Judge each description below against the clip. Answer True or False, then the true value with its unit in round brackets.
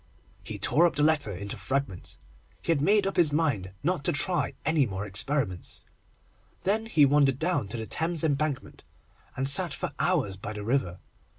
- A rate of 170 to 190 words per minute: True (180 wpm)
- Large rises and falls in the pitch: True (7.2 semitones)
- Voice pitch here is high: False (140 Hz)